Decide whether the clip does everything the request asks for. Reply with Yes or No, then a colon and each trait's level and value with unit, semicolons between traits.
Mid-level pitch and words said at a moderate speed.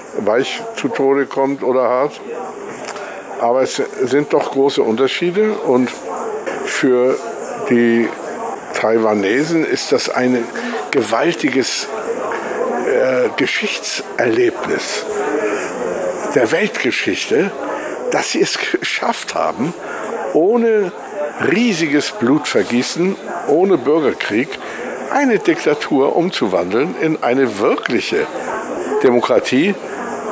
No: medium, 145 Hz; slow, 80 wpm